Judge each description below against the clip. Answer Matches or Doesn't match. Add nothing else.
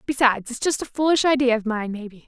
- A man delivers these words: Doesn't match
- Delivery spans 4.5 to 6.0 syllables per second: Doesn't match